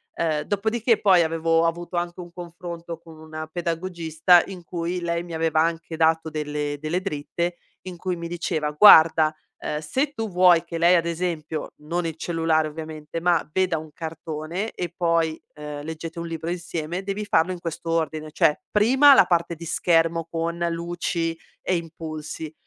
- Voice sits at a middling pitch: Yes, medium, 165 Hz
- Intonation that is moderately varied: No, narrow, 1.6 semitones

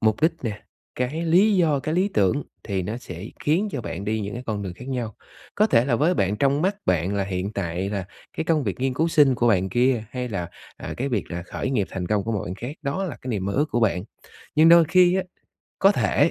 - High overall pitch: No, low, 120 Hz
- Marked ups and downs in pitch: Yes, wide, 7.4 semitones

